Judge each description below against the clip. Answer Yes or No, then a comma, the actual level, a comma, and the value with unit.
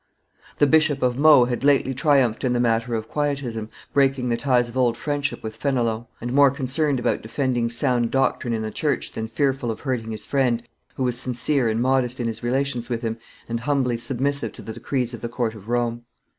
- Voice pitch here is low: Yes, low, 125 Hz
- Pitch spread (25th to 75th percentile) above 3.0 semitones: No, average, 2.7 semitones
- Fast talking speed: Yes, fast, 210 wpm